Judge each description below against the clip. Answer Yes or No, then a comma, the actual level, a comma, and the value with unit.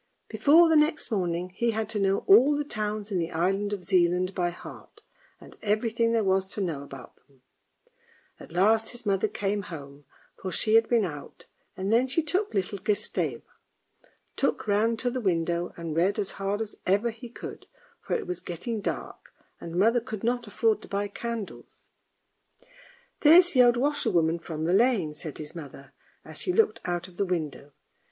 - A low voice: No, high, 205 Hz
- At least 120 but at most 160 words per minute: No, average, 185 wpm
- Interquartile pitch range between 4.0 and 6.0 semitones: Yes, average, 4.8 semitones